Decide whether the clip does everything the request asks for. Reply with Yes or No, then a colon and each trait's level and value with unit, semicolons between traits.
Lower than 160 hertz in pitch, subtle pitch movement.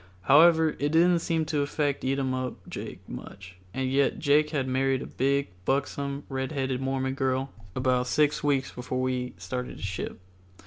Yes: low, 135 Hz; narrow, 2.0 semitones